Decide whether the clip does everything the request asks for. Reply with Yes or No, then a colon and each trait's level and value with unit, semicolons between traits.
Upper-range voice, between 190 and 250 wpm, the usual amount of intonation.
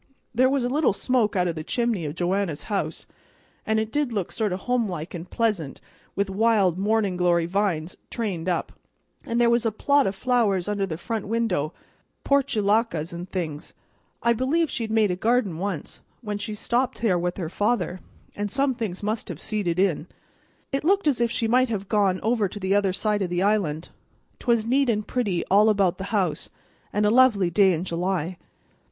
Yes: high, 205 Hz; average, 195 wpm; average, 4.4 semitones